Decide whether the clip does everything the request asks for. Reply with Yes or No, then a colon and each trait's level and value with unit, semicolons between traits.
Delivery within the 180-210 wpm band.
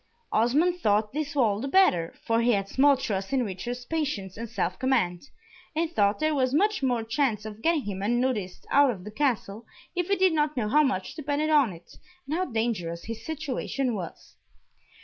Yes: average, 190 wpm